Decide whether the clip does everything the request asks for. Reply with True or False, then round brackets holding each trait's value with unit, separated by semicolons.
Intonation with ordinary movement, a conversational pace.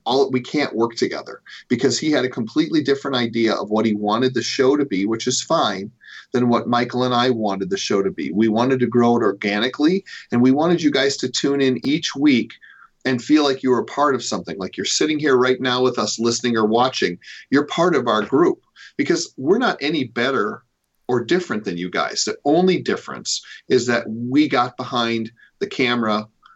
False (3.0 semitones; 210 wpm)